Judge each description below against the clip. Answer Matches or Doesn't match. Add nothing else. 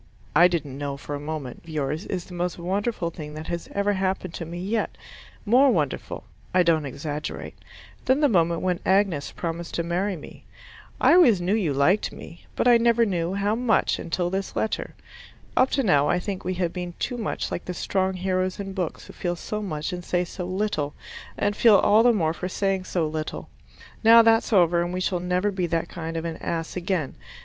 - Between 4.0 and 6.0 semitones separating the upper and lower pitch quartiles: Doesn't match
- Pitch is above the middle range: Doesn't match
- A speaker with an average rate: Doesn't match